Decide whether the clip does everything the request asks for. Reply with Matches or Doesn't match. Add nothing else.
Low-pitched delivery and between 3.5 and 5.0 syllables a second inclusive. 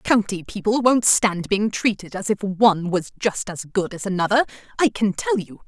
Doesn't match